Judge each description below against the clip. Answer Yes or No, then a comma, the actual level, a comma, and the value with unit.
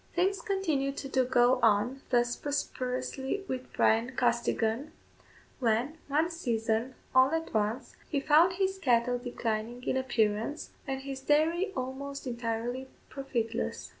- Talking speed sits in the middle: No, slow, 125 wpm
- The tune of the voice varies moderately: Yes, average, 3.4 semitones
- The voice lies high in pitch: Yes, very high, 260 Hz